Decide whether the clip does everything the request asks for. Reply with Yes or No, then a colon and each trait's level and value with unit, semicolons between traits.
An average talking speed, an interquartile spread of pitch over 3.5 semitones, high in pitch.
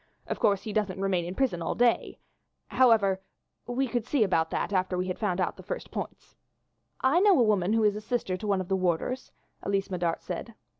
No: fast, 215 wpm; average, 4.2 semitones; high, 200 Hz